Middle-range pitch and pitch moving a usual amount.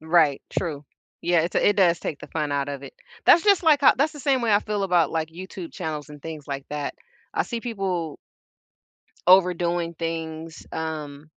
Yes: medium, 165 Hz; average, 4.0 semitones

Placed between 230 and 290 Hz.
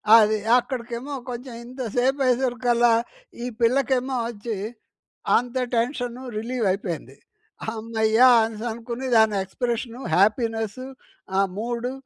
Yes: high, 235 Hz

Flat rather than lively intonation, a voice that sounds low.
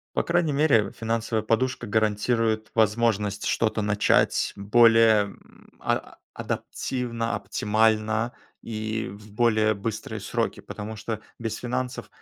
Yes: narrow, 1.6 semitones; low, 110 Hz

